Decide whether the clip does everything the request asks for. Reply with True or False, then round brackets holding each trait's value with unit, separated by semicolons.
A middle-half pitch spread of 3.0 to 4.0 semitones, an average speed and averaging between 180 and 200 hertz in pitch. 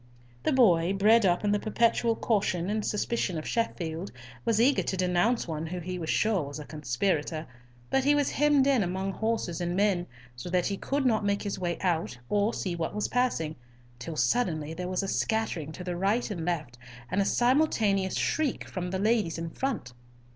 False (4.7 semitones; 195 wpm; 190 Hz)